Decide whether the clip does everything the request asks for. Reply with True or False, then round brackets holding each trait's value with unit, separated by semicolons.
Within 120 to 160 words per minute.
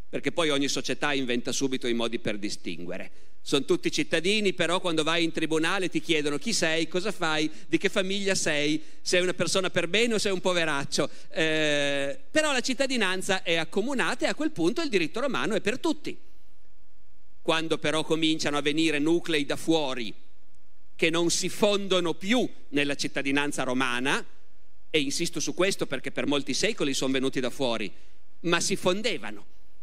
False (170 wpm)